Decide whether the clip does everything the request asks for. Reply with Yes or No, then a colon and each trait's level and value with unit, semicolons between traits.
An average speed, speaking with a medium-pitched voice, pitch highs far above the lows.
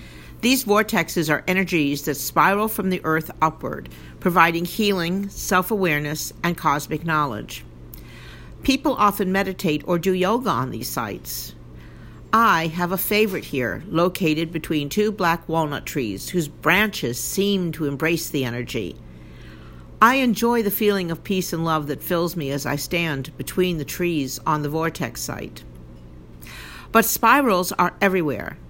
Yes: average, 145 wpm; medium, 165 Hz; wide, 5.9 semitones